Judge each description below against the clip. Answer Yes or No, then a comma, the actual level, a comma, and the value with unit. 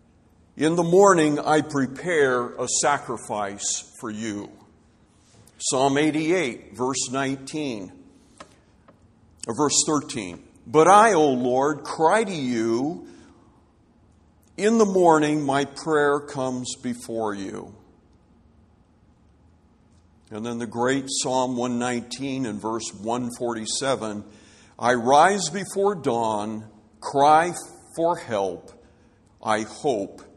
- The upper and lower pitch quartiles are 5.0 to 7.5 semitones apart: Yes, wide, 5.4 semitones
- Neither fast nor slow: No, slow, 95 wpm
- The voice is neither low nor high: No, low, 125 Hz